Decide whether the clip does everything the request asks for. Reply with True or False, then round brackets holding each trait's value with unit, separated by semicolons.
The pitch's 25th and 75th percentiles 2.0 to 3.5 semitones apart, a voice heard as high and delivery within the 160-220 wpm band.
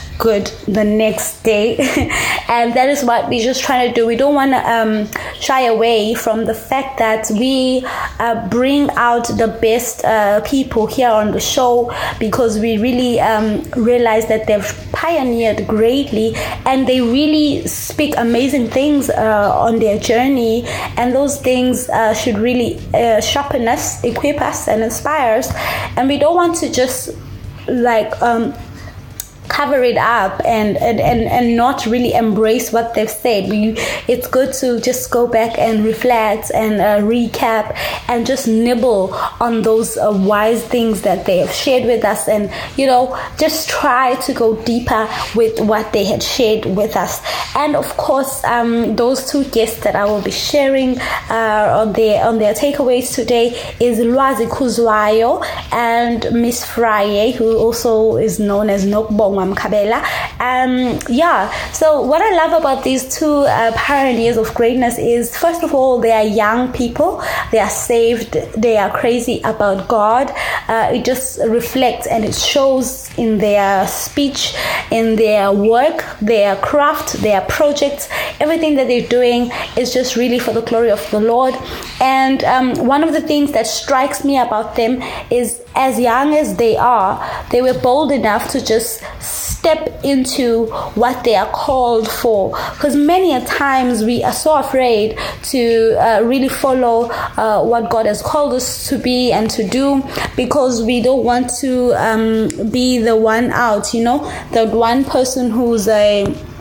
True (2.9 semitones; 240 Hz; 165 wpm)